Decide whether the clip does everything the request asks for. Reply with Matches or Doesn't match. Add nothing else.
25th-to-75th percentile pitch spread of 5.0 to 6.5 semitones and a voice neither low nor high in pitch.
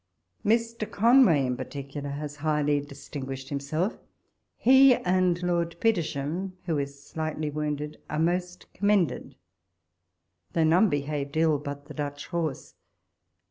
Doesn't match